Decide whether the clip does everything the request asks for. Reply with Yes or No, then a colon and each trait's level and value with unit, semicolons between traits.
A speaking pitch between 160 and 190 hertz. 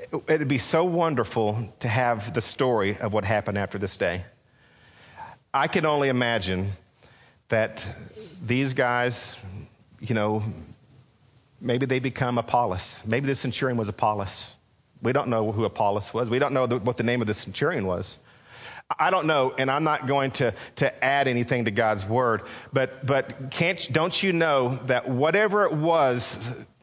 No: low, 125 Hz